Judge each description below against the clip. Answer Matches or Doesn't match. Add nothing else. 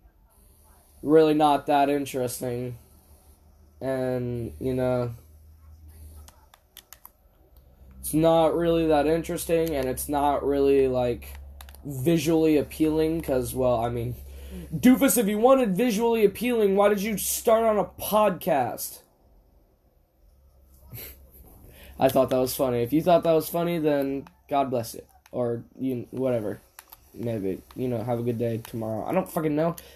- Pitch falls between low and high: Doesn't match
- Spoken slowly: Matches